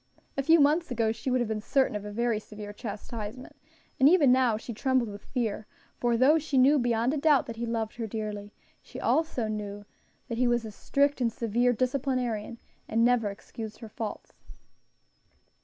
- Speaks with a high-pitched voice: Yes, high, 235 Hz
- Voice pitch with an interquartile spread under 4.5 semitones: Yes, average, 3.3 semitones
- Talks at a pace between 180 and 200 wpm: Yes, average, 190 wpm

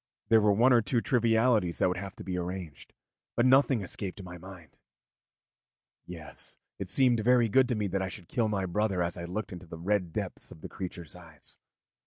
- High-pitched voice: No, very low, 95 Hz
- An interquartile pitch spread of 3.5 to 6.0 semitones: Yes, average, 4.3 semitones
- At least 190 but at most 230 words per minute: Yes, fast, 205 wpm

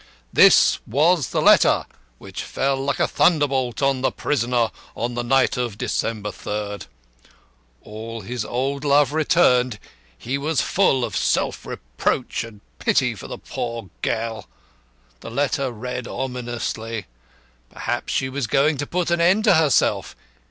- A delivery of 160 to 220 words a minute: No, average, 145 wpm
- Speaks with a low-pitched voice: Yes, low, 125 Hz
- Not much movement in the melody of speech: No, average, 3.6 semitones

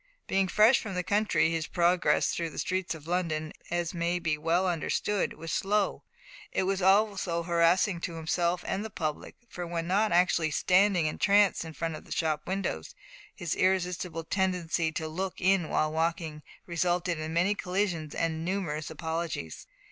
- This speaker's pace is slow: No, average, 165 wpm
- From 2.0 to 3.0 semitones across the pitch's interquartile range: Yes, narrow, 2.6 semitones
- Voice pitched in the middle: Yes, medium, 175 Hz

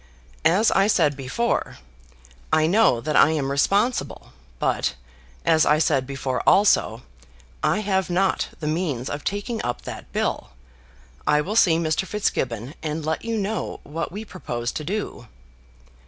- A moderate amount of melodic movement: No, wide, 6.3 semitones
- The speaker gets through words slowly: No, average, 150 wpm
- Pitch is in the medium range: Yes, medium, 160 Hz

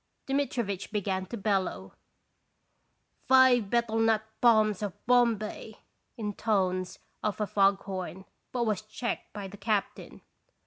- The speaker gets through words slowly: Yes, slow, 125 wpm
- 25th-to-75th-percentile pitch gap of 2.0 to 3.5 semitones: Yes, average, 3.0 semitones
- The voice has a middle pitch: No, high, 210 Hz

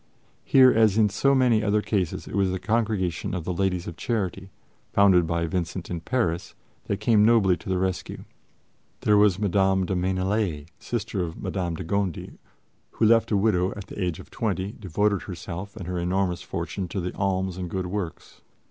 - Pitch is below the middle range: Yes, very low, 95 Hz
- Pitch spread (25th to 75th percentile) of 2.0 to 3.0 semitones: Yes, average, 2.7 semitones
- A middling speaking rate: Yes, average, 185 wpm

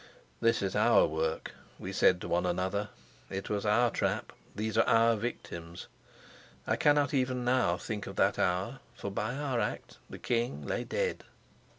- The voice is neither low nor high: No, low, 110 Hz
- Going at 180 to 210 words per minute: No, average, 170 wpm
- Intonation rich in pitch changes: No, average, 4.3 semitones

